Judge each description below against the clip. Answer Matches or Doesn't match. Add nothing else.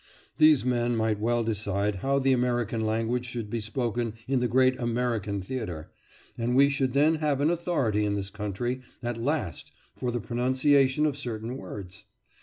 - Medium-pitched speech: Doesn't match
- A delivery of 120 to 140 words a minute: Doesn't match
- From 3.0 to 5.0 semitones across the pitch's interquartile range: Matches